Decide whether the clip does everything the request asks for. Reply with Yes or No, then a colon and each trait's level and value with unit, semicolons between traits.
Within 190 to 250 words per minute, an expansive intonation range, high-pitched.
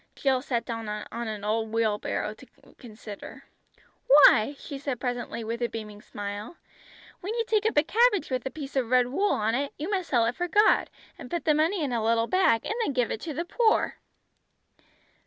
Yes: fast, 205 wpm; wide, 6.2 semitones; very high, 255 Hz